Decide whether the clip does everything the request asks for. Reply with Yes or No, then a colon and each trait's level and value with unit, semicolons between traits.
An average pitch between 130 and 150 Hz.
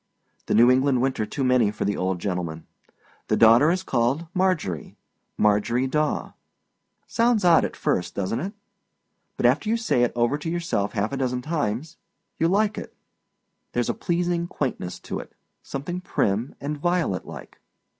Yes: low, 135 Hz